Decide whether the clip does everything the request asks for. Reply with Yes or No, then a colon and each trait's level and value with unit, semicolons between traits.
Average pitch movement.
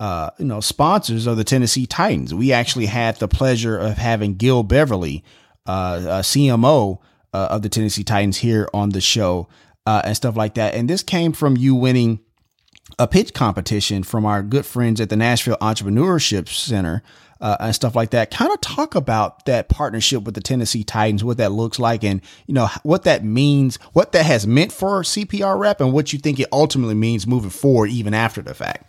Yes: average, 3.7 semitones